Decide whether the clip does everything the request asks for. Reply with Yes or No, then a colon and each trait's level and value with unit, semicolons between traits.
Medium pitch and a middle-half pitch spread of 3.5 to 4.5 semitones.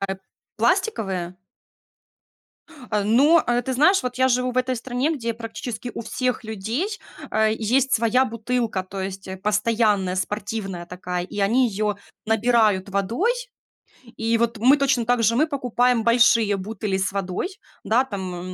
No: high, 225 Hz; average, 3.9 semitones